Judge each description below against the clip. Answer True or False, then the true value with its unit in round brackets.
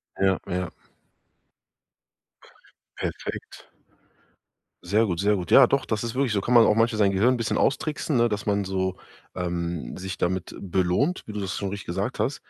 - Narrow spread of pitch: False (3.7 semitones)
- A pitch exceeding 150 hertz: False (100 Hz)